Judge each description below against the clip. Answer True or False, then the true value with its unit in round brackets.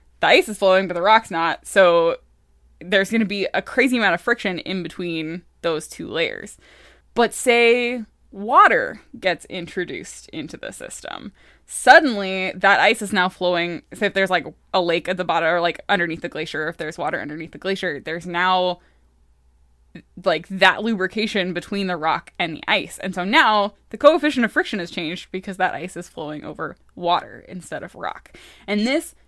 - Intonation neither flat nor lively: True (4.2 semitones)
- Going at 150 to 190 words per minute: True (185 wpm)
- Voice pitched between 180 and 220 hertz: True (185 Hz)